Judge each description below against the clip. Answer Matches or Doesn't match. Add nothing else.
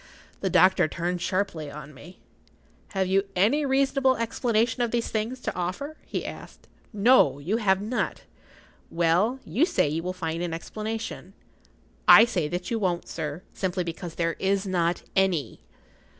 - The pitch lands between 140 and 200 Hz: Matches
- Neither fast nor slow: Matches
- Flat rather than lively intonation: Doesn't match